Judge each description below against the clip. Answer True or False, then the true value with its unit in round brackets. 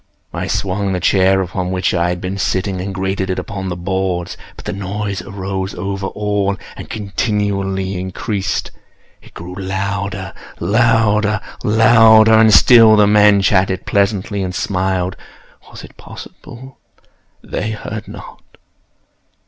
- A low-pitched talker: True (100 Hz)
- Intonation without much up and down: True (1.8 semitones)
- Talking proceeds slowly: True (130 wpm)